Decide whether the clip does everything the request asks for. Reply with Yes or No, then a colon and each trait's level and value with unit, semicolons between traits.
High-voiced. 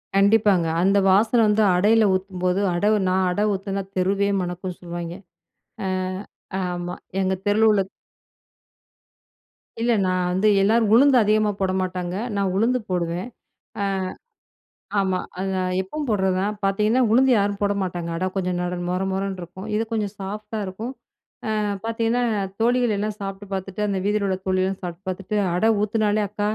Yes: high, 195 Hz